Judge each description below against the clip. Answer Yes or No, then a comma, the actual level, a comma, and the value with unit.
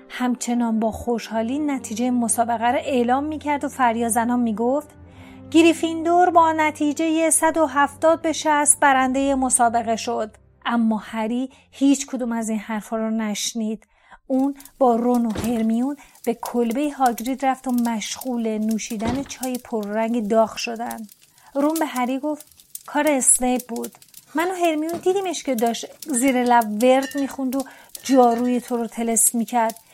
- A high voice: Yes, very high, 250 Hz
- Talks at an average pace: Yes, average, 140 wpm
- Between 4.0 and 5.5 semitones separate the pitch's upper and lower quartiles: No, average, 3.5 semitones